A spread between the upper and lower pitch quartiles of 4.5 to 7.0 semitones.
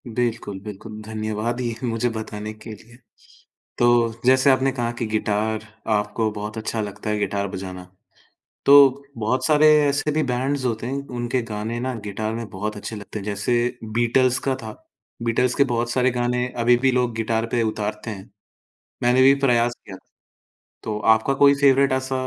No: average, 2.9 semitones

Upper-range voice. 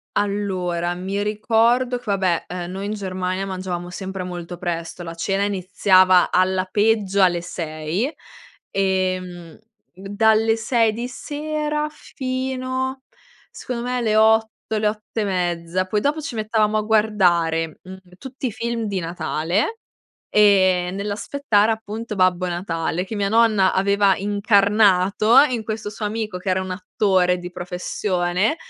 Yes: high, 200 Hz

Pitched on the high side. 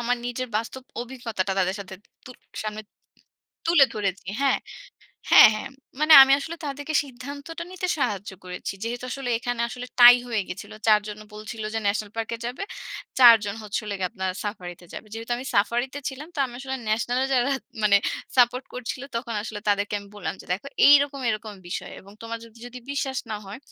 Yes: high, 235 Hz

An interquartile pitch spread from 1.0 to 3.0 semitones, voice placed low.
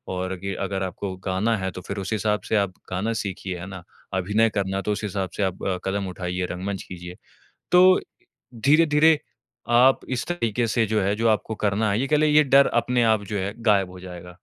No: average, 3.4 semitones; low, 100 Hz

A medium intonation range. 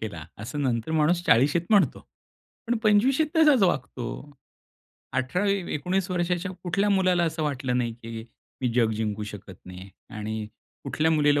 No: wide, 8.0 semitones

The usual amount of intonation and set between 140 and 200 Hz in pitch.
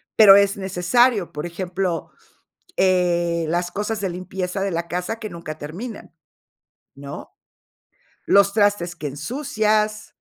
Yes: average, 3.4 semitones; medium, 185 Hz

